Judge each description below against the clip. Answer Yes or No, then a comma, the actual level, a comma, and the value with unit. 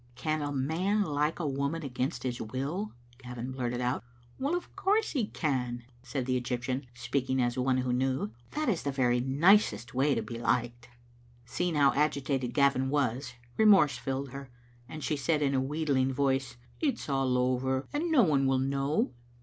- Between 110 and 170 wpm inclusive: No, average, 190 wpm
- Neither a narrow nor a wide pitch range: Yes, average, 3.1 semitones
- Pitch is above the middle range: No, low, 135 Hz